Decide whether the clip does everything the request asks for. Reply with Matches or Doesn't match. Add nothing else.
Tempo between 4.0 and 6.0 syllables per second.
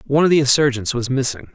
Doesn't match